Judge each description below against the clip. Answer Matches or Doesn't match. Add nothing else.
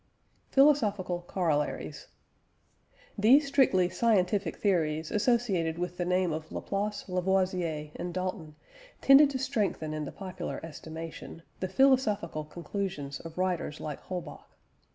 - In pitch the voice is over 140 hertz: Matches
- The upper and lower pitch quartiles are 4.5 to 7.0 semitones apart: Doesn't match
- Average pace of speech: Doesn't match